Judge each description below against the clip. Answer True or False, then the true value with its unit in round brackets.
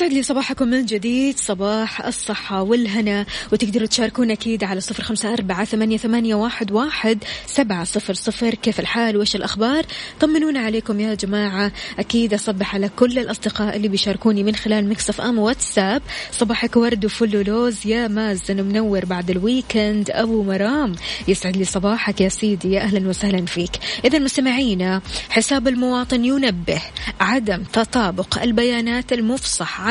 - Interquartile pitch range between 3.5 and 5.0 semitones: False (2.7 semitones)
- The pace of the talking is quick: True (140 wpm)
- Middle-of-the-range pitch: False (220 Hz)